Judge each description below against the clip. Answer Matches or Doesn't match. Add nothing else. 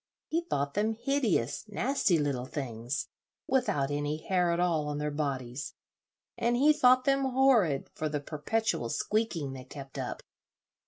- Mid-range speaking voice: Matches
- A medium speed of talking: Matches